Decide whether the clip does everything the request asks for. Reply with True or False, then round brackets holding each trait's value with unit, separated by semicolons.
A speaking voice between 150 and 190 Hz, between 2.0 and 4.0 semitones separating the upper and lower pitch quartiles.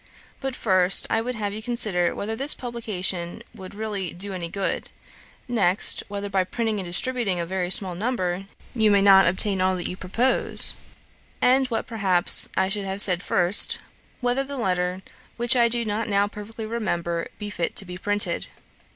False (200 Hz; 3.6 semitones)